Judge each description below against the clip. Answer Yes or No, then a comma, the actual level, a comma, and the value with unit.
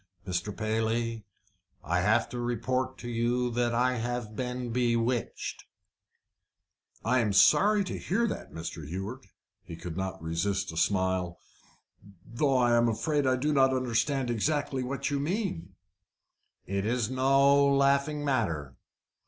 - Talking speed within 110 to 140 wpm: Yes, slow, 135 wpm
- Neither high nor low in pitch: No, low, 120 Hz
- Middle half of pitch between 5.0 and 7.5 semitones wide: No, average, 4.5 semitones